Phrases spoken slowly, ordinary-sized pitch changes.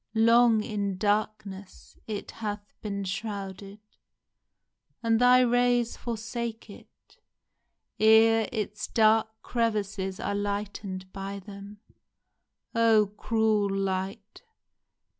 No: slow, 90 wpm; narrow, 2.1 semitones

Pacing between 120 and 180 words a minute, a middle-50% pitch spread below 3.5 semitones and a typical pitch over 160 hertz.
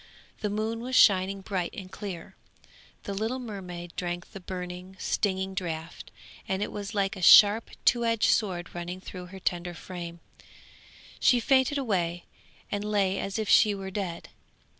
Yes: average, 160 wpm; average, 2.8 semitones; high, 190 Hz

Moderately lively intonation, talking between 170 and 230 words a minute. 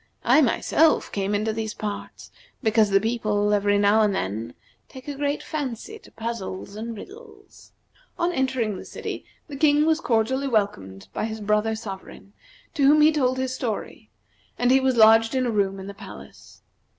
Yes: average, 4.6 semitones; average, 175 wpm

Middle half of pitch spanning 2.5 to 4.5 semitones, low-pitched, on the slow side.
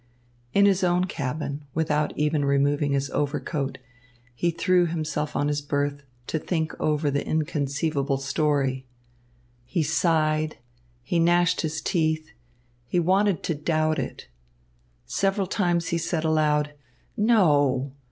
No: average, 2.9 semitones; medium, 155 Hz; slow, 125 wpm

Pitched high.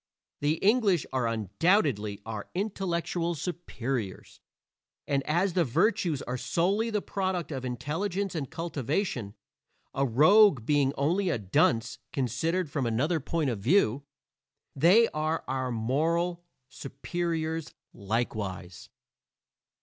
No: medium, 150 Hz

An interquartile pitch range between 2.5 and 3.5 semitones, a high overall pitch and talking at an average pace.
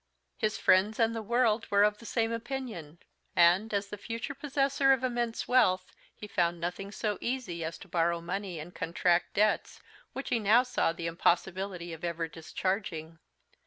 No: average, 5.1 semitones; high, 200 Hz; average, 170 wpm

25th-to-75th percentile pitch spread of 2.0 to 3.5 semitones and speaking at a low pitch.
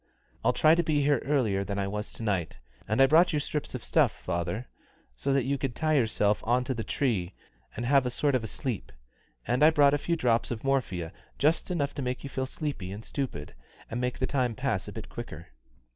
No: average, 4.7 semitones; low, 125 Hz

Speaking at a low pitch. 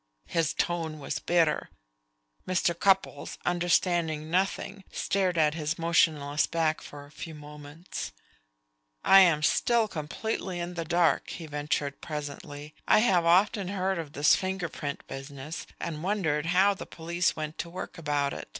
No: medium, 165 Hz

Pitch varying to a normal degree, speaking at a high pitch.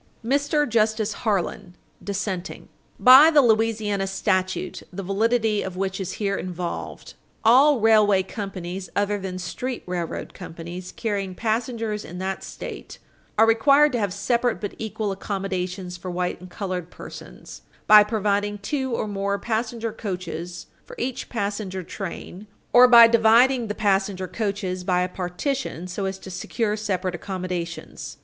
Yes: average, 3.5 semitones; high, 200 Hz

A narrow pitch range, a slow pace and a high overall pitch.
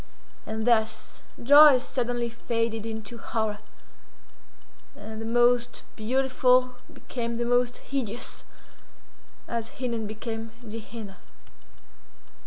Yes: narrow, 1.8 semitones; slow, 95 wpm; high, 235 Hz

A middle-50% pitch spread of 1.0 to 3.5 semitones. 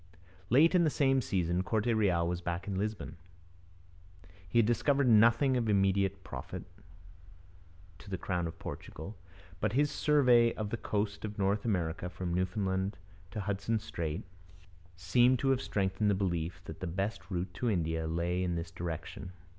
No: average, 4.3 semitones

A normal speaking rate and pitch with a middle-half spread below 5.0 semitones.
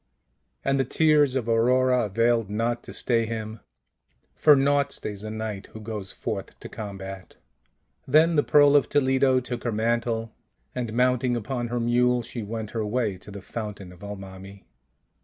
Yes: average, 165 wpm; average, 3.2 semitones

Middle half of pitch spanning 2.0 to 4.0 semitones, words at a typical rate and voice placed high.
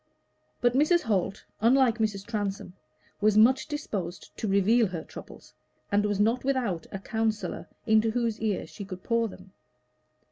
Yes: average, 2.9 semitones; average, 150 wpm; high, 215 Hz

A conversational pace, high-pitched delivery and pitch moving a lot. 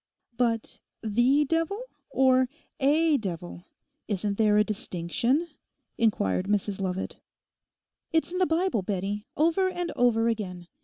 No: slow, 120 wpm; high, 230 Hz; wide, 7.1 semitones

